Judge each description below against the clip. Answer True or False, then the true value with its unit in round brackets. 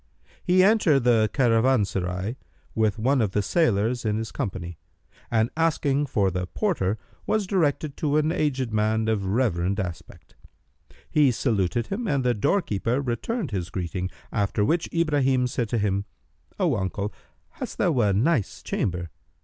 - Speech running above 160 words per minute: False (150 wpm)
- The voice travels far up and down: True (6.3 semitones)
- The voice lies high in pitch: False (115 Hz)